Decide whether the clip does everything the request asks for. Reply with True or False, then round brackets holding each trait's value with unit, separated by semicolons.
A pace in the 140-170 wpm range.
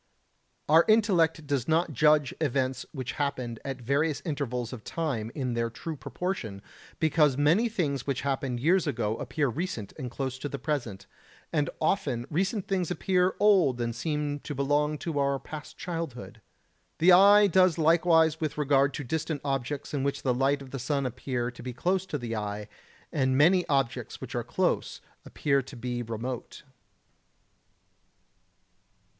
True (160 wpm)